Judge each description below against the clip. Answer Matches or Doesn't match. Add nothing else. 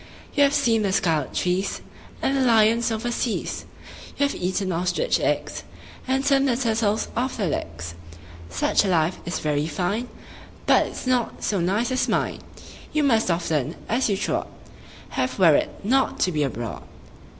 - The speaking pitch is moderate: Doesn't match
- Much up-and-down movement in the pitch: Matches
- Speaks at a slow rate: Doesn't match